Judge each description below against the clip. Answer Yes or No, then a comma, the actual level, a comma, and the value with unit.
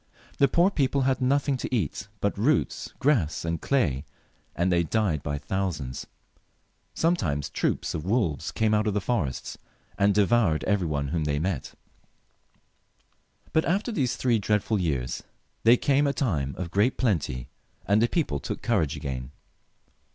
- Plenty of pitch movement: Yes, wide, 8.7 semitones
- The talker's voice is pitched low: Yes, low, 100 Hz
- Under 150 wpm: No, average, 155 wpm